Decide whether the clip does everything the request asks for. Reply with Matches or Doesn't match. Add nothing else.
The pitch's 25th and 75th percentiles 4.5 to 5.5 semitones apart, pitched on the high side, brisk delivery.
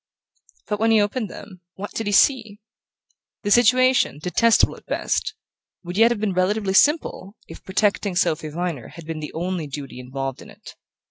Doesn't match